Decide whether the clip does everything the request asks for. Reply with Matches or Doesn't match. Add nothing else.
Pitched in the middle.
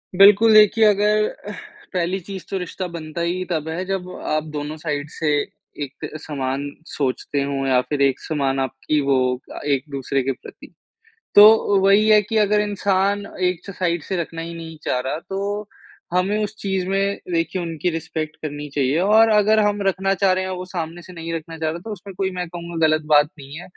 Matches